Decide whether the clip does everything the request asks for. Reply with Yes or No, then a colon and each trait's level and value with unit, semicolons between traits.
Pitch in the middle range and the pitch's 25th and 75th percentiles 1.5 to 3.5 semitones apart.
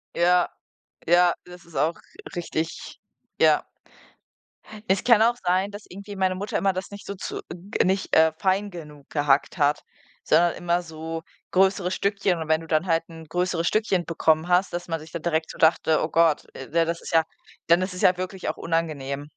Yes: medium, 175 Hz; narrow, 2.6 semitones